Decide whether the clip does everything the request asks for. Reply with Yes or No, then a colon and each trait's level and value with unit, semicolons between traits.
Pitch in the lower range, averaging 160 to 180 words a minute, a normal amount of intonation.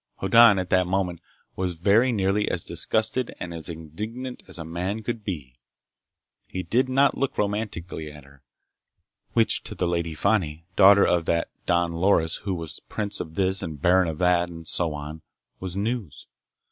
Yes: very low, 90 Hz; average, 170 wpm; average, 3.8 semitones